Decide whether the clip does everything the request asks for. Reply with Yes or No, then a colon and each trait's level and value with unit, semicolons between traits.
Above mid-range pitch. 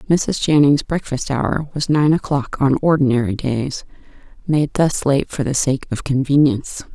No: medium, 140 Hz